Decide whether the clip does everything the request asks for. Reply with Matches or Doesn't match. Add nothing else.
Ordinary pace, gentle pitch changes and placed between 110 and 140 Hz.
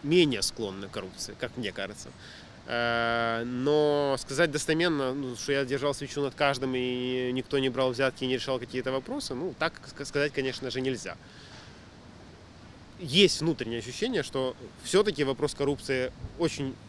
Matches